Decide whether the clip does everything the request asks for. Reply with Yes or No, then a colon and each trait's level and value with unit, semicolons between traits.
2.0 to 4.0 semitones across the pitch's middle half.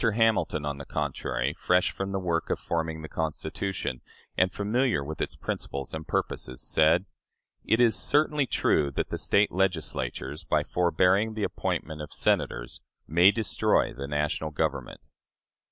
No: average, 4.8 semitones